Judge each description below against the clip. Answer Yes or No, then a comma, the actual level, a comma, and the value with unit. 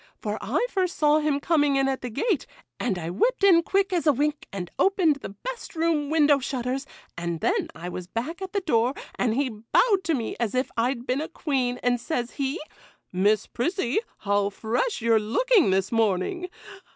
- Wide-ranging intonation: Yes, wide, 6.5 semitones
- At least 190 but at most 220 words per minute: Yes, average, 195 wpm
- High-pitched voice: Yes, very high, 270 Hz